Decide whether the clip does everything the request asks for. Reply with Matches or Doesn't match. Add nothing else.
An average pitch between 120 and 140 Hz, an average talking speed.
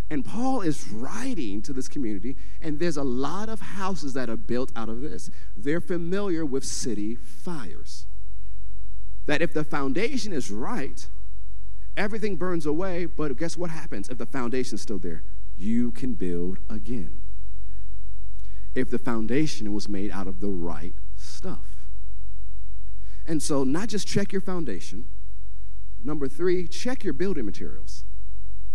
Doesn't match